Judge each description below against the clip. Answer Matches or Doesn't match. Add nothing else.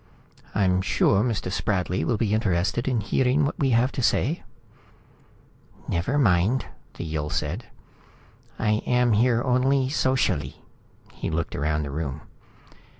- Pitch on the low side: Matches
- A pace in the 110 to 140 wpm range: Matches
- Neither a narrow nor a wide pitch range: Doesn't match